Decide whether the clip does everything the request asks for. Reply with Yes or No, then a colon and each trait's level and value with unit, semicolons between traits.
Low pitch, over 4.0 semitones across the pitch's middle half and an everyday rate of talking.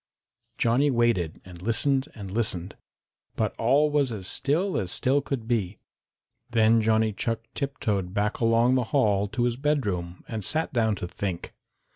Yes: low, 115 Hz; average, 4.5 semitones; average, 155 wpm